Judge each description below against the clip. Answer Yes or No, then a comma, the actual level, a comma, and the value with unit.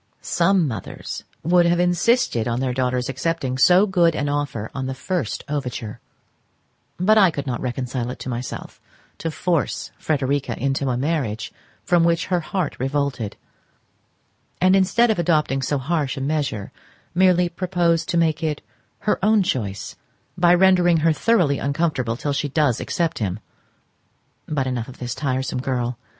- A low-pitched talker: No, medium, 145 Hz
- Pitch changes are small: No, average, 5.3 semitones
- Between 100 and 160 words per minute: Yes, average, 155 wpm